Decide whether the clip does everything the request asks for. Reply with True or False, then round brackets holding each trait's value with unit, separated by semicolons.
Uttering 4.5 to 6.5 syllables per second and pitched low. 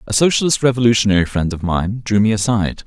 False (6.7 syllables/s; 110 Hz)